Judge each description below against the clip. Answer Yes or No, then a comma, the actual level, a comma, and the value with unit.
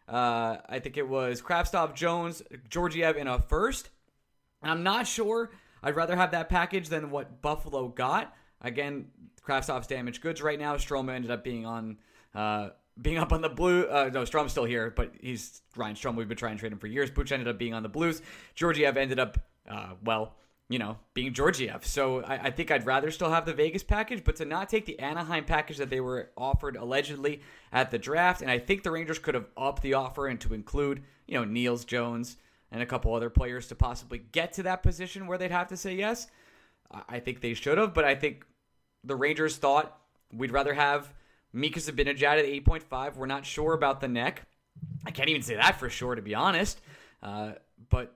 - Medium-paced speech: No, fast, 215 wpm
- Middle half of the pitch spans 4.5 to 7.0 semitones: Yes, average, 5.0 semitones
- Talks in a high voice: No, medium, 140 Hz